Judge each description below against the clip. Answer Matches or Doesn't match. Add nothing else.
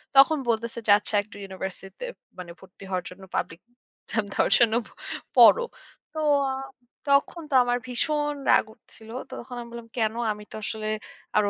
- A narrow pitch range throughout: Doesn't match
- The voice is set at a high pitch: Matches